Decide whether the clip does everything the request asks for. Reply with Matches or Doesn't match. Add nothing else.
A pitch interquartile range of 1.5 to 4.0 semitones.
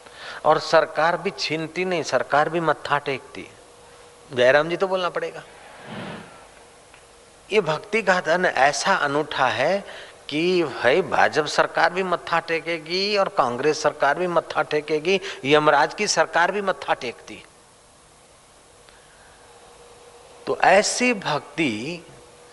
Matches